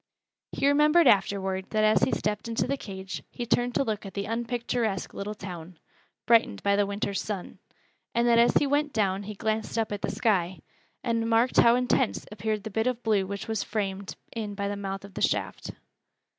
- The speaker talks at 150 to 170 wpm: No, average, 200 wpm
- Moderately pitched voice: No, high, 215 Hz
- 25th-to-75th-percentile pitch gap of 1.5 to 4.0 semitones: Yes, average, 2.8 semitones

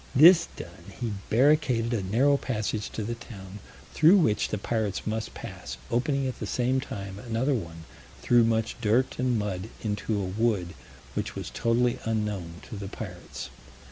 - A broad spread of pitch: No, average, 3.6 semitones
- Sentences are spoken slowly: No, average, 165 wpm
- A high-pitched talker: No, low, 115 Hz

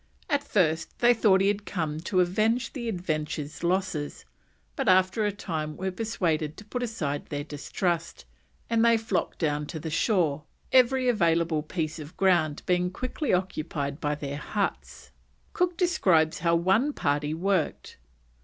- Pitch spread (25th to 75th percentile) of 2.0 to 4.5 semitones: No, wide, 5.4 semitones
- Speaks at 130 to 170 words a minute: Yes, average, 155 wpm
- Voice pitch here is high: No, medium, 180 Hz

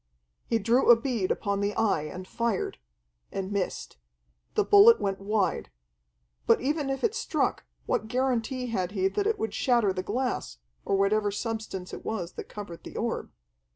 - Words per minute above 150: Yes, average, 170 wpm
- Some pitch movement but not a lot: Yes, average, 4.3 semitones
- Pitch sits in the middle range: No, high, 220 Hz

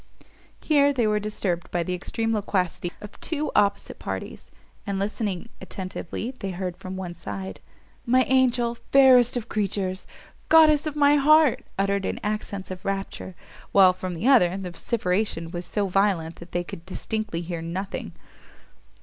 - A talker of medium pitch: No, high, 195 Hz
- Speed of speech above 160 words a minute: No, average, 150 wpm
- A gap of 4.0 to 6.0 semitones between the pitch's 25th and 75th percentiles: Yes, average, 4.7 semitones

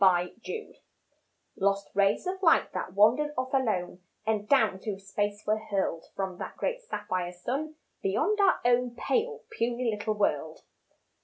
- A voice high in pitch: Yes, high, 215 Hz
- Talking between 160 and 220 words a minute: No, average, 145 wpm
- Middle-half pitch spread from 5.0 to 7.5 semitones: Yes, wide, 5.6 semitones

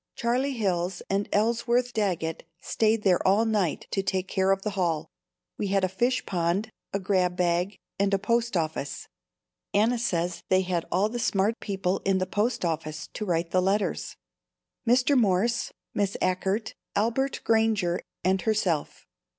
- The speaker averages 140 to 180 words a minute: Yes, average, 160 wpm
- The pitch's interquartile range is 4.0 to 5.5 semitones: No, average, 3.6 semitones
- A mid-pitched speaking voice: No, high, 195 Hz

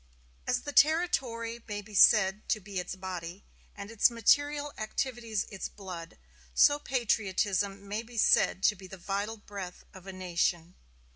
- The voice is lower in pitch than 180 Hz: No, high, 205 Hz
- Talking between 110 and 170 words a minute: Yes, average, 155 wpm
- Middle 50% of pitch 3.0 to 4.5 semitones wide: Yes, average, 3.4 semitones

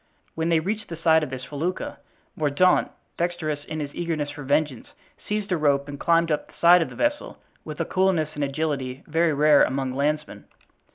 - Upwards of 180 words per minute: Yes, average, 190 wpm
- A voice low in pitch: No, medium, 155 Hz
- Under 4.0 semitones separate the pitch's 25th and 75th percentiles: Yes, average, 2.9 semitones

